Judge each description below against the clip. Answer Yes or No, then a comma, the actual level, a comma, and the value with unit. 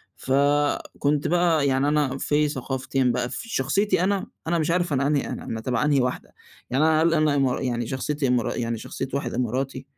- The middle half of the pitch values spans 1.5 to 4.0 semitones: Yes, average, 2.9 semitones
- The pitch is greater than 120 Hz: Yes, medium, 140 Hz